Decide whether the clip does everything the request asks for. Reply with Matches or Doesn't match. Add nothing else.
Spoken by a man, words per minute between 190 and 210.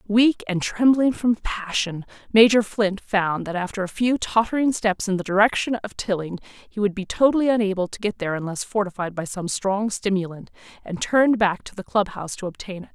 Doesn't match